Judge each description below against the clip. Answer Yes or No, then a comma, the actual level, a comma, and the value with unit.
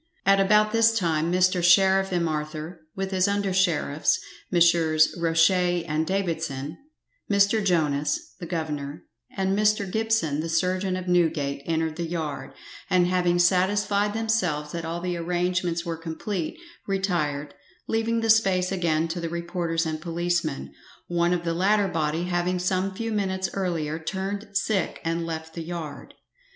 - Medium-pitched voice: Yes, medium, 175 Hz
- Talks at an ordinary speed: Yes, average, 145 wpm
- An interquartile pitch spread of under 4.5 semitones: Yes, average, 2.9 semitones